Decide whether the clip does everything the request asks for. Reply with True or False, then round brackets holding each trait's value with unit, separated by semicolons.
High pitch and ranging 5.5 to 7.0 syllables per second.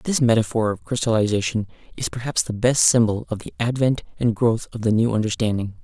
False (115 Hz; 5.7 syllables/s)